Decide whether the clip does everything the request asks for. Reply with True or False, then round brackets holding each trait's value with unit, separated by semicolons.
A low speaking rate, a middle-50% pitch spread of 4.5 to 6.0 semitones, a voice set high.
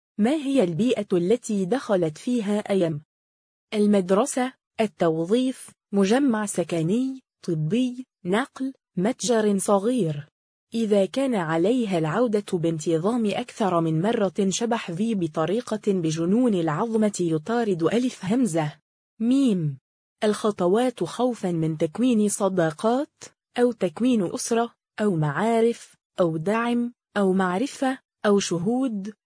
True (100 wpm; 5.1 semitones; 210 Hz)